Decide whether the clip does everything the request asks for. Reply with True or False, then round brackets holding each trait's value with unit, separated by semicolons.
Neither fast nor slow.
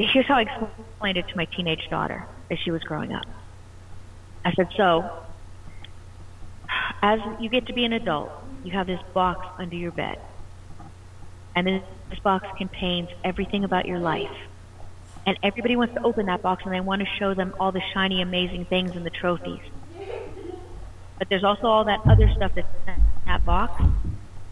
True (175 wpm)